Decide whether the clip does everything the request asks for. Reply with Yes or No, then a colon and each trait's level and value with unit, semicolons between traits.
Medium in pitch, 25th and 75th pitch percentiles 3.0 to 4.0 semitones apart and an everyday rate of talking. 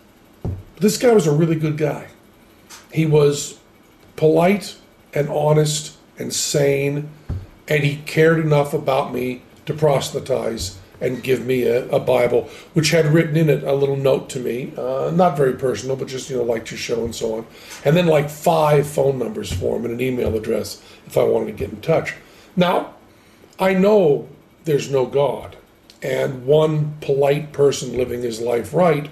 Yes: medium, 145 Hz; average, 3.4 semitones; average, 175 wpm